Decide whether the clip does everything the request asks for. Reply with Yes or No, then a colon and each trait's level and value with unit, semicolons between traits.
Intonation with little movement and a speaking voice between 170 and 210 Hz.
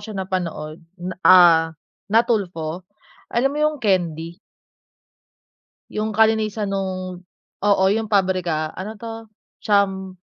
No: average, 3.2 semitones; high, 190 Hz